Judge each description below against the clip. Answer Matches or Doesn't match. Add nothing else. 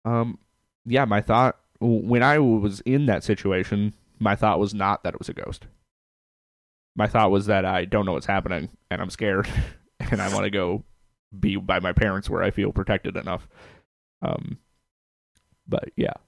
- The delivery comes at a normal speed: Matches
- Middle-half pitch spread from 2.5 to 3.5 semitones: Matches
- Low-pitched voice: Matches